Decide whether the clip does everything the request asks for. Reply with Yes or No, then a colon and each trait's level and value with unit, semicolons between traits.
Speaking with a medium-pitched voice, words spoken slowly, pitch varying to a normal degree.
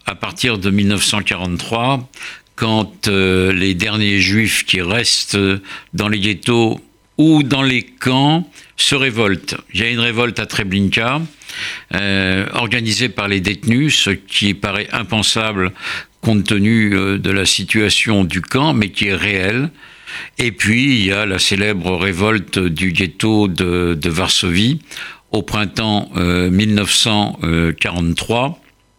No: low, 105 Hz; slow, 135 wpm; average, 3.5 semitones